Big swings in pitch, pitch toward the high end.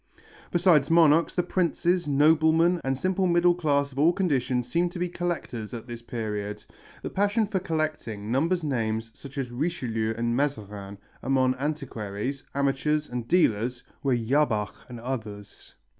No: wide, 6.2 semitones; medium, 140 Hz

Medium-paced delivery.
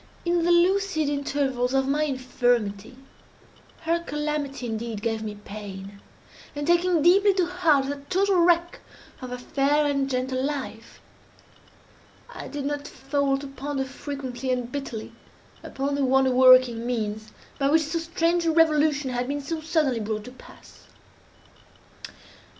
Yes: average, 145 wpm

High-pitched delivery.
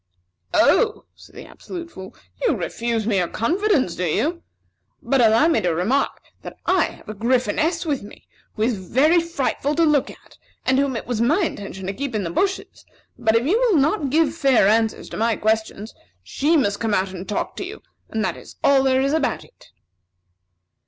Yes: very high, 260 Hz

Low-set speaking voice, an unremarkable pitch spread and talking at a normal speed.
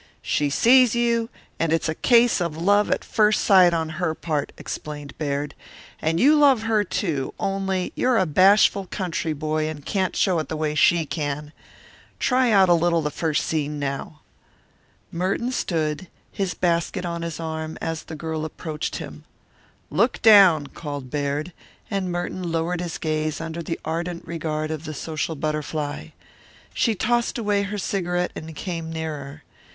No: medium, 165 Hz; average, 3.8 semitones; average, 160 wpm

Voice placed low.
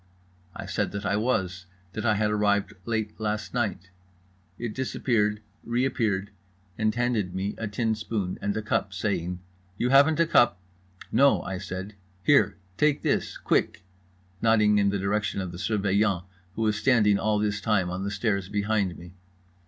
Yes: low, 105 Hz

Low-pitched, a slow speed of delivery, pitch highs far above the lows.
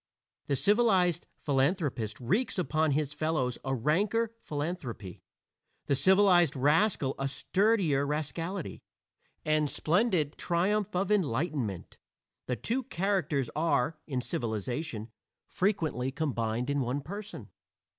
No: medium, 155 Hz; slow, 105 wpm; wide, 5.9 semitones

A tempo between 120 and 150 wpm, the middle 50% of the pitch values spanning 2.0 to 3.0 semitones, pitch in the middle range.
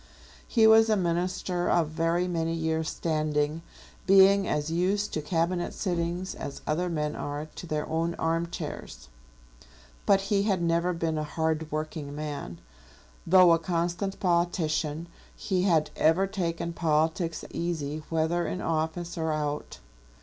Yes: average, 140 wpm; narrow, 2.4 semitones; medium, 165 Hz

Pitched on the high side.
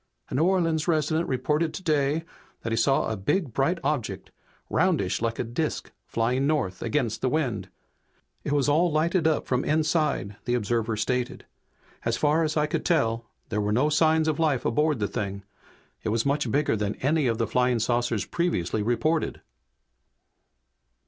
No: low, 135 Hz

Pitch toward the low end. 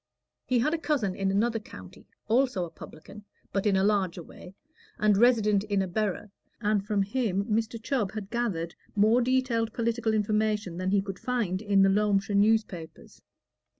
No: high, 210 Hz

